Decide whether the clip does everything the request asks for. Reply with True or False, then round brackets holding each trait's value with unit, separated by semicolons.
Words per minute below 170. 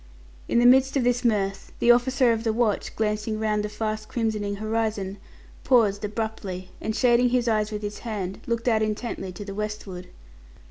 False (180 wpm)